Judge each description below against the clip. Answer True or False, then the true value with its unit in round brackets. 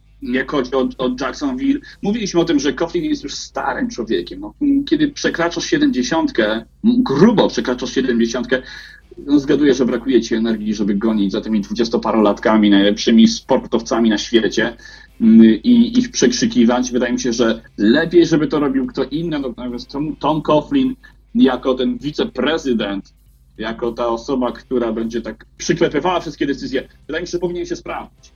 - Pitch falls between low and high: False (130 Hz)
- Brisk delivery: False (150 wpm)